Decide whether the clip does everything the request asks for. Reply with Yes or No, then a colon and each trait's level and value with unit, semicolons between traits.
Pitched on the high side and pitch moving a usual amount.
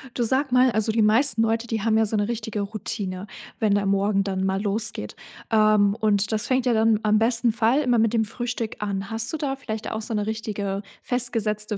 No: high, 220 Hz; narrow, 2.0 semitones